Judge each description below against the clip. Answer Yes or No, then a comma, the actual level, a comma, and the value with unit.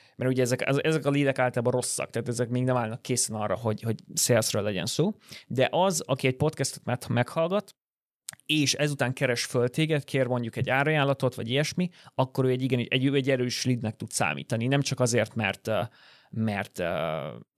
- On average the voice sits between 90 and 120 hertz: No, low, 130 Hz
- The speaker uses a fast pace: Yes, fast, 190 wpm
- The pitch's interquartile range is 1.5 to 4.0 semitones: Yes, average, 2.8 semitones